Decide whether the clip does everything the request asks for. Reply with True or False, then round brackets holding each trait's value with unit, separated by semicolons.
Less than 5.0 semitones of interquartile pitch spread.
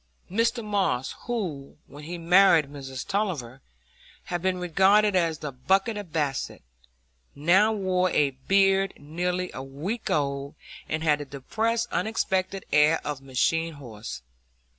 False (5.4 semitones)